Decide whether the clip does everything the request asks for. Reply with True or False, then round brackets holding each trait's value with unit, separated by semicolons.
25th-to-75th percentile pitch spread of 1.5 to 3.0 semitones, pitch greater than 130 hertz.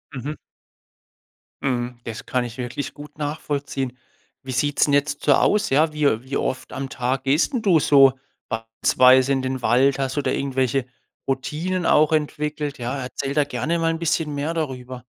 True (2.7 semitones; 140 Hz)